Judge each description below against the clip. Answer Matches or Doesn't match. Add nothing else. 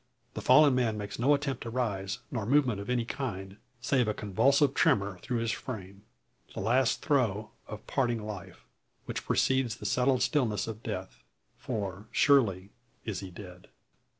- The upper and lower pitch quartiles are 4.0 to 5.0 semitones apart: Matches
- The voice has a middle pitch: Doesn't match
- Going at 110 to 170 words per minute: Matches